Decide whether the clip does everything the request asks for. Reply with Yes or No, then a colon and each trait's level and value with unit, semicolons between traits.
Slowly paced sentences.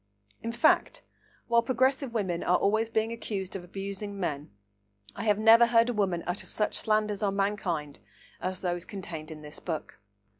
No: average, 165 wpm